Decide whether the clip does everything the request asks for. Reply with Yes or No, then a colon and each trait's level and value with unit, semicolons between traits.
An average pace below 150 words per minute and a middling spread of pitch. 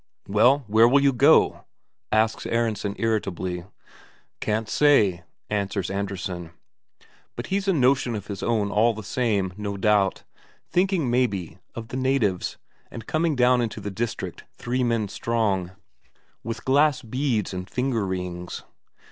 Yes: average, 140 wpm; average, 4.2 semitones